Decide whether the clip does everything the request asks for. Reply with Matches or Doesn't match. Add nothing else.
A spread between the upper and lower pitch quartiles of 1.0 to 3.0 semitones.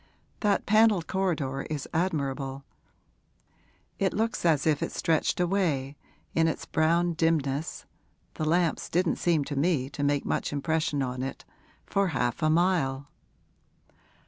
Doesn't match